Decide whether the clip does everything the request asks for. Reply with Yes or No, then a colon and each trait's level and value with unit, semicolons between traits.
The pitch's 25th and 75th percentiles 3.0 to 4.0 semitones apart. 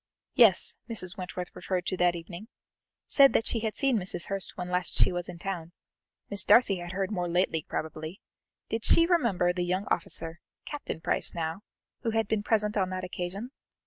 Yes: average, 3.4 semitones